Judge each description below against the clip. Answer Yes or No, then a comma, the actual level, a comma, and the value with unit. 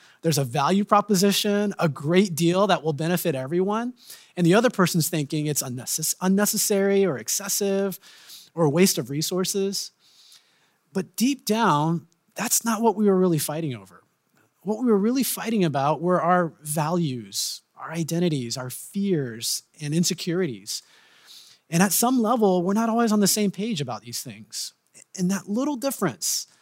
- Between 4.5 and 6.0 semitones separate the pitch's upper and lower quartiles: Yes, average, 4.8 semitones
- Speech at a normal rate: Yes, average, 155 wpm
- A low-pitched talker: No, medium, 180 Hz